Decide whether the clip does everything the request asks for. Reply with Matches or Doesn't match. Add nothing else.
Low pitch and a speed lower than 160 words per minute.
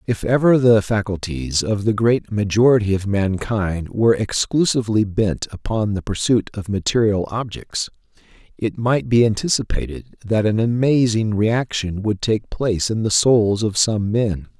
Matches